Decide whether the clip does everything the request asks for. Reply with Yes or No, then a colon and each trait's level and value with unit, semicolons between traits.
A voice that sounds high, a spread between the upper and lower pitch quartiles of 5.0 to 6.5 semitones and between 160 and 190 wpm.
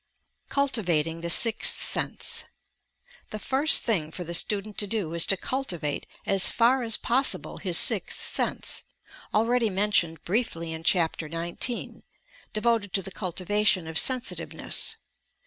No: high, 195 Hz; average, 5.3 semitones; average, 140 wpm